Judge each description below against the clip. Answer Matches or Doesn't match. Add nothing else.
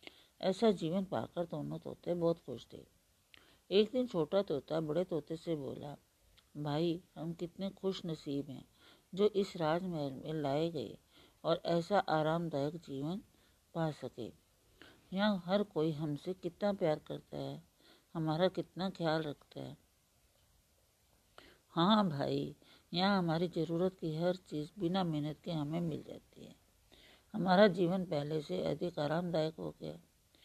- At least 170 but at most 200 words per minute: Doesn't match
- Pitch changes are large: Doesn't match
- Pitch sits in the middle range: Matches